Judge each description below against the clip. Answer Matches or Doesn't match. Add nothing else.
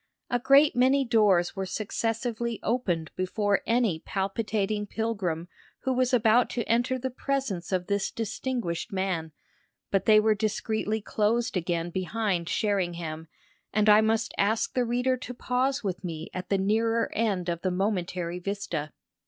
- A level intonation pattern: Doesn't match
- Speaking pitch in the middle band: Doesn't match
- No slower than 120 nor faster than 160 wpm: Matches